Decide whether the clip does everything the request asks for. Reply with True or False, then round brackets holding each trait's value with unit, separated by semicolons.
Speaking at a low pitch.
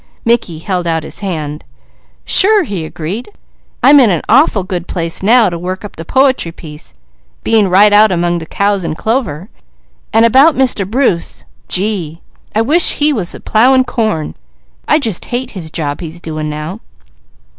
False (195 Hz)